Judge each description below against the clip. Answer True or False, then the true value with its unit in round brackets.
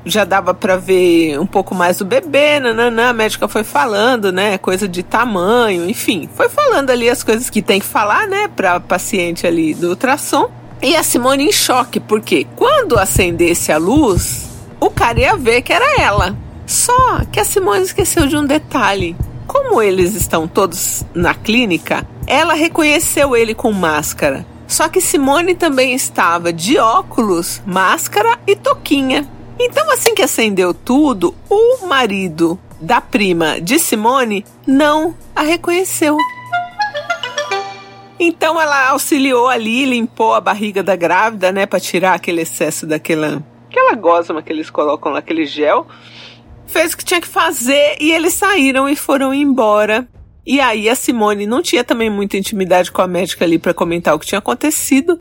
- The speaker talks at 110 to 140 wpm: False (160 wpm)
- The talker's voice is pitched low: False (245 Hz)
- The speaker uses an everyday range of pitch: False (8.9 semitones)